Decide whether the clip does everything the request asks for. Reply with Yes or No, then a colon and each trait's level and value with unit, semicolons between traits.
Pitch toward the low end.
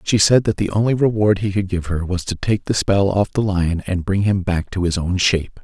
Yes: very low, 95 Hz